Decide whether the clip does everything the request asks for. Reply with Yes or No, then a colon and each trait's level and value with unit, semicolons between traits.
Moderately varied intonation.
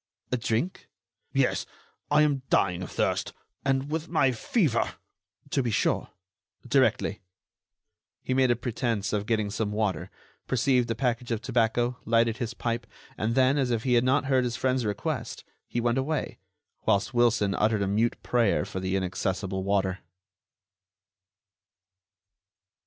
Yes: average, 3.7 semitones